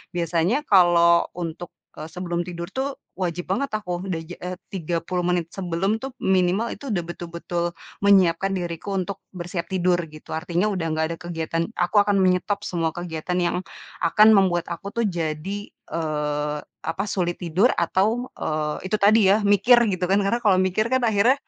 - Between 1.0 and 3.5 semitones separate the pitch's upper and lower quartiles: Yes, average, 2.9 semitones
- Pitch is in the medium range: Yes, medium, 180 Hz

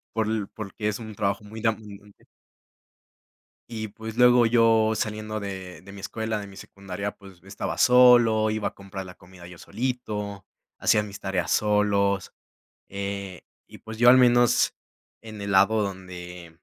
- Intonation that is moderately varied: No, narrow, 2.2 semitones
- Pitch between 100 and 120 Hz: Yes, low, 105 Hz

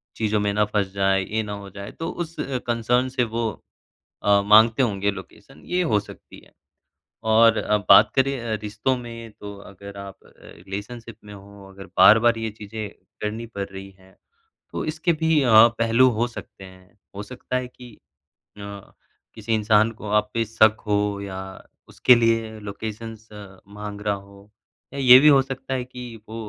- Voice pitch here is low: Yes, low, 110 Hz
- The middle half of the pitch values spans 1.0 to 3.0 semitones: Yes, average, 2.7 semitones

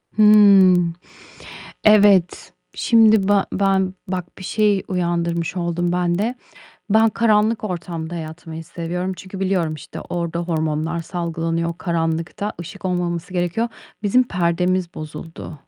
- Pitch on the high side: No, medium, 180 Hz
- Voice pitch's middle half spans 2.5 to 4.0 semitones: Yes, average, 2.8 semitones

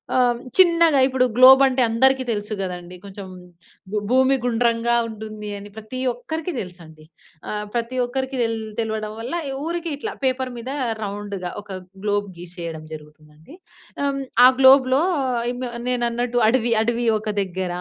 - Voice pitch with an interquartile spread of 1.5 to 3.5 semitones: No, average, 4.3 semitones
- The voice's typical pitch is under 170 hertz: No, high, 230 Hz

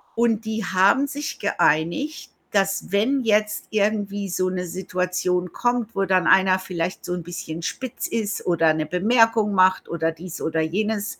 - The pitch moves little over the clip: No, average, 3.5 semitones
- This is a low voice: No, high, 195 Hz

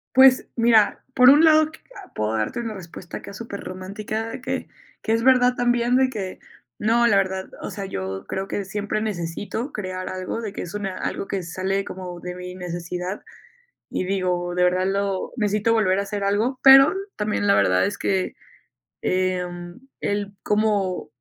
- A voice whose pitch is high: Yes, high, 200 Hz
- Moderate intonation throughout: Yes, average, 3.4 semitones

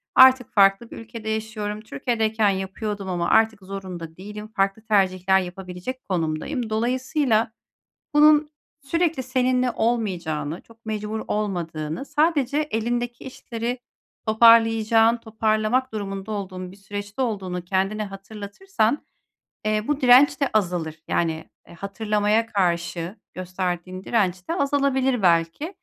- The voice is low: No, high, 215 Hz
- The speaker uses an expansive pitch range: No, average, 4.2 semitones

